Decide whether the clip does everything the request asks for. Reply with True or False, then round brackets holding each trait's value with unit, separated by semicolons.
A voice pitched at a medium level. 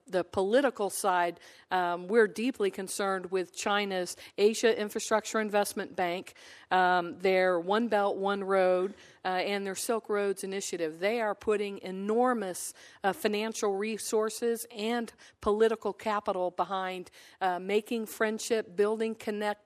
False (205 Hz)